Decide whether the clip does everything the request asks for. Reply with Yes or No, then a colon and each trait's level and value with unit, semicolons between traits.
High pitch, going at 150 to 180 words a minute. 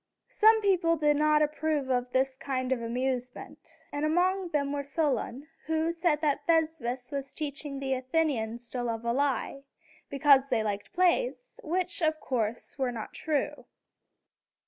Yes: very high, 285 Hz; average, 155 wpm